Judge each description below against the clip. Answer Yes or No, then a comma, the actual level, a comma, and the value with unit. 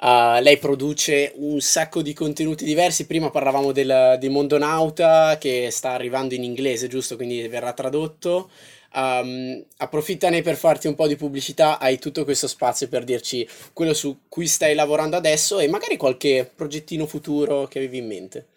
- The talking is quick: No, average, 160 wpm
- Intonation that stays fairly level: No, average, 3.2 semitones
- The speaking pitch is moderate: Yes, medium, 145 Hz